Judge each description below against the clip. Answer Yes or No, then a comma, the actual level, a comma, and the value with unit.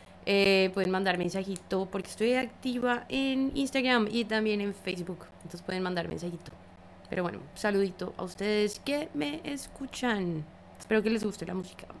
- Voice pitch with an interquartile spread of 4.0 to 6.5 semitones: Yes, average, 5.0 semitones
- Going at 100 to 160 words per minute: Yes, average, 155 wpm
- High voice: Yes, high, 195 Hz